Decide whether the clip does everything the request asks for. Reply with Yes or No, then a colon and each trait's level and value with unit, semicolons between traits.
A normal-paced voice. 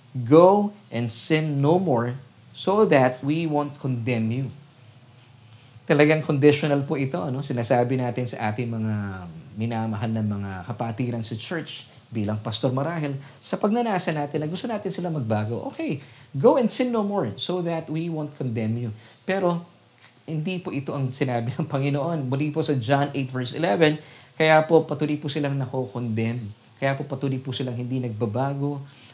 No: fast, 165 wpm